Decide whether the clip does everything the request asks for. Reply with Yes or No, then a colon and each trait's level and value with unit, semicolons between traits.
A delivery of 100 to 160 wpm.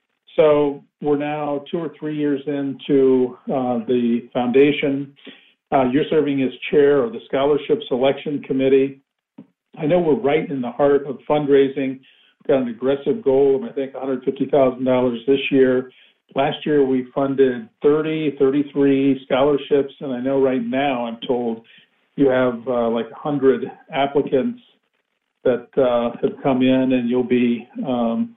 Yes: average, 150 wpm